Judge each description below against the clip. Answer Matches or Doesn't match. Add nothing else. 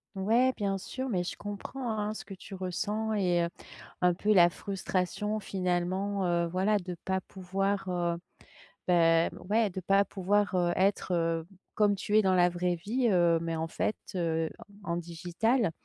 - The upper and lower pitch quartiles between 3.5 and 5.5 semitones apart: Doesn't match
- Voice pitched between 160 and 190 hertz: Matches